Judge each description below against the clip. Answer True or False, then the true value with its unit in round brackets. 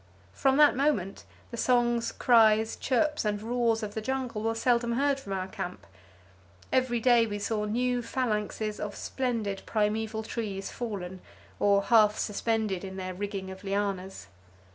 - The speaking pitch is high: True (220 Hz)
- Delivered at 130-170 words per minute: True (145 wpm)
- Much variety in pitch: False (3.1 semitones)